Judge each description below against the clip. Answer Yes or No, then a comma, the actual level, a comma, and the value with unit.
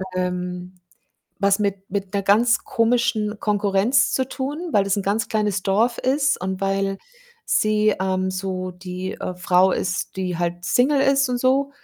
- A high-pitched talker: Yes, high, 200 Hz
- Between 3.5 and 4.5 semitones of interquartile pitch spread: Yes, average, 4.0 semitones